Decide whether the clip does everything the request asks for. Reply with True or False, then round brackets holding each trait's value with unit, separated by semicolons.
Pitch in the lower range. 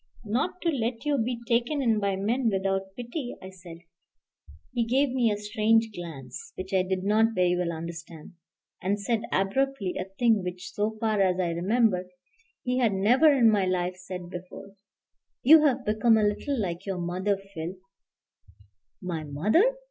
False (200 Hz)